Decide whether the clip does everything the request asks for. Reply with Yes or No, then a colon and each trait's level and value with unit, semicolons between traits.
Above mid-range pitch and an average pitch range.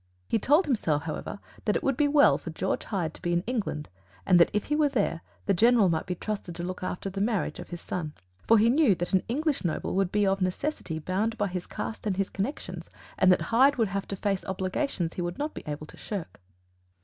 Yes: high, 195 Hz; average, 4.7 semitones